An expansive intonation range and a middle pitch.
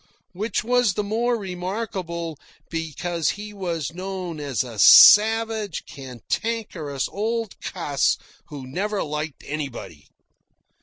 Yes: wide, 5.9 semitones; medium, 180 Hz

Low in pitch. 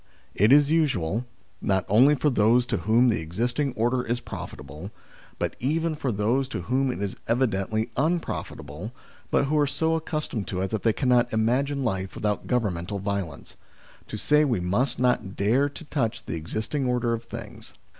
Yes: low, 120 Hz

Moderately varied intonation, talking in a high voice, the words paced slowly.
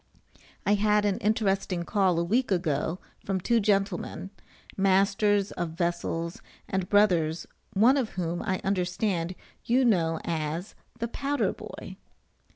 Yes: average, 3.4 semitones; high, 195 Hz; slow, 130 wpm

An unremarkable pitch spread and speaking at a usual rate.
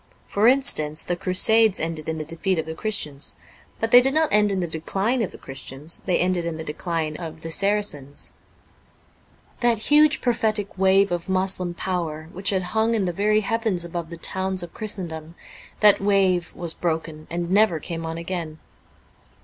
Yes: average, 4.2 semitones; average, 180 wpm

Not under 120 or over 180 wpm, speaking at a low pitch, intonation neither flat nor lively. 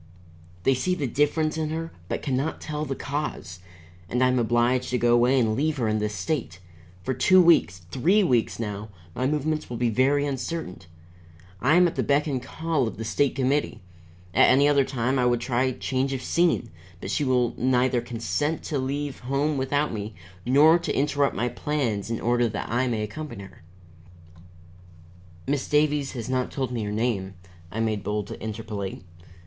No: average, 190 wpm; low, 130 Hz; average, 4.0 semitones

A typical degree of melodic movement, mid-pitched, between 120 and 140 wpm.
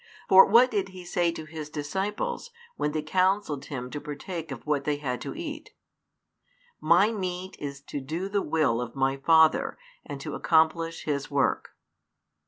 No: average, 4.7 semitones; medium, 160 Hz; average, 170 wpm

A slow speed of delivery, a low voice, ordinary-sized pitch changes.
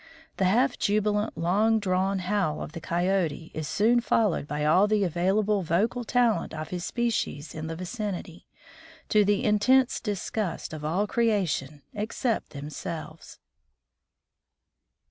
No: slow, 130 wpm; high, 195 Hz; average, 4.6 semitones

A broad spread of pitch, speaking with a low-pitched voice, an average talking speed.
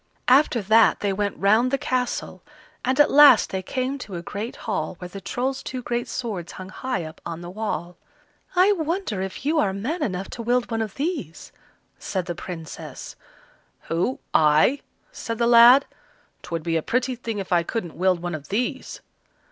No: wide, 5.9 semitones; high, 220 Hz; average, 185 wpm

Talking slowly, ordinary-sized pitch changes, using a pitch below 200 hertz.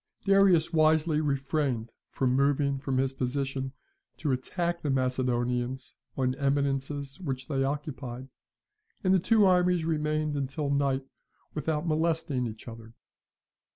Yes: slow, 120 wpm; average, 3.0 semitones; medium, 140 Hz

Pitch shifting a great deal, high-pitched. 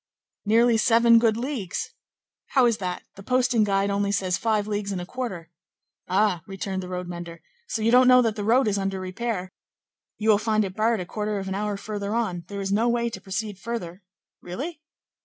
No: average, 3.3 semitones; high, 210 Hz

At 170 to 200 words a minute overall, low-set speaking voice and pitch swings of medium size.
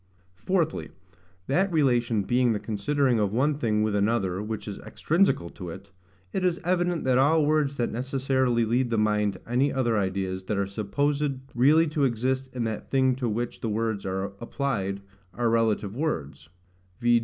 Yes: average, 175 wpm; low, 120 Hz; average, 4.9 semitones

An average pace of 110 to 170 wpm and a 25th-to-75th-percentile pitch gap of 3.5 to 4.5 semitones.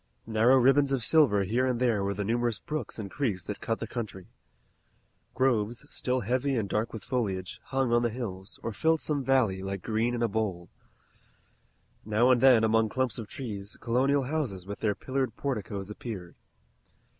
No: average, 180 wpm; average, 4.0 semitones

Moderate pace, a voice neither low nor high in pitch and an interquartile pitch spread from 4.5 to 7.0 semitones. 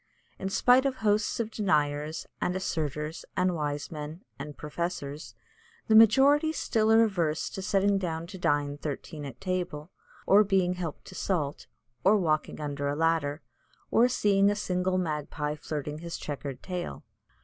Yes: average, 155 wpm; medium, 170 Hz; average, 4.9 semitones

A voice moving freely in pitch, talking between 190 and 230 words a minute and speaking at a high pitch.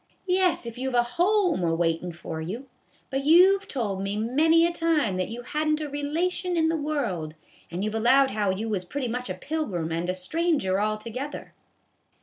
Yes: wide, 8.4 semitones; average, 200 wpm; very high, 250 Hz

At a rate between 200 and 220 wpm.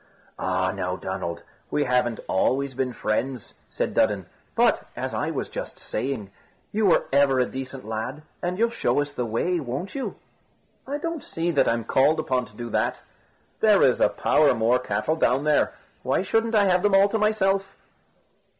No: average, 180 wpm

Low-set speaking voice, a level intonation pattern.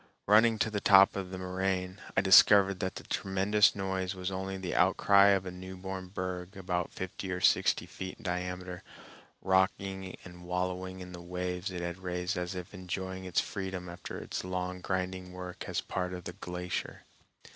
Yes: very low, 95 Hz; narrow, 1.0 semitones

